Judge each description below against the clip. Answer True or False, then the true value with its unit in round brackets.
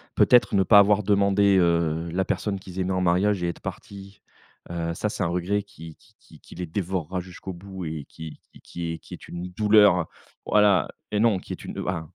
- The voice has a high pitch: False (95 Hz)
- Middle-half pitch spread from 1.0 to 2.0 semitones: False (2.8 semitones)